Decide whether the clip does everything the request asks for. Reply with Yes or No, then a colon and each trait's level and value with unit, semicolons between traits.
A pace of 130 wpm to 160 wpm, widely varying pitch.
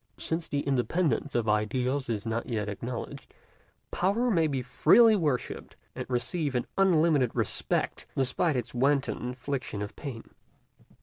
No: slow, 135 wpm; average, 5.0 semitones